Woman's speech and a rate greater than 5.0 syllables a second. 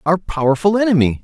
No: male; 6.3 syllables/s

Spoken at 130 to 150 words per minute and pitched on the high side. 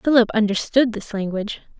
Yes: slow, 135 wpm; high, 220 Hz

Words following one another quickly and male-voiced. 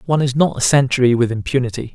Yes: fast, 215 wpm; male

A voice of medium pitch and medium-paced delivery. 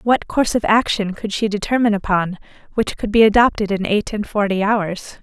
No: high, 210 Hz; average, 195 wpm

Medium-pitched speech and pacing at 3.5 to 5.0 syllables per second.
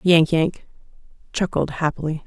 Yes: medium, 165 Hz; 4.6 syllables/s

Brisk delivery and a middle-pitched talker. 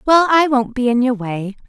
No: fast, 250 wpm; very high, 250 Hz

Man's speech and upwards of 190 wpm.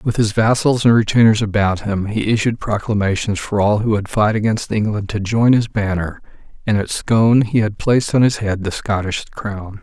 Yes: male; average, 200 wpm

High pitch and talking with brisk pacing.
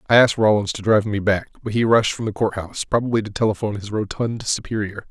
No: low, 105 Hz; fast, 225 wpm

